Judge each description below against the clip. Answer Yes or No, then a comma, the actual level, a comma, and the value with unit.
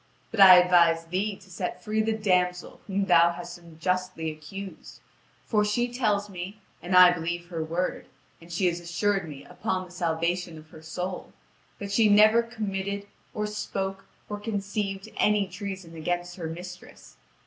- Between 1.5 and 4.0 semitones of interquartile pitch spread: Yes, average, 2.8 semitones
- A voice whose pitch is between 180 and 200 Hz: Yes, medium, 185 Hz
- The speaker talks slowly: No, average, 160 wpm